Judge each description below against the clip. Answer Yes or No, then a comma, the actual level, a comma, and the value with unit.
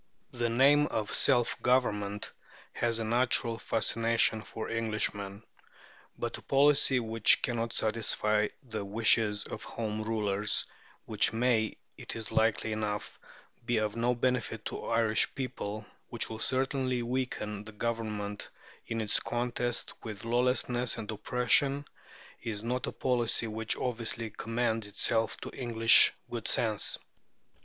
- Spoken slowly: Yes, slow, 130 wpm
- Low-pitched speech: Yes, low, 115 Hz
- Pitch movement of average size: No, narrow, 2.2 semitones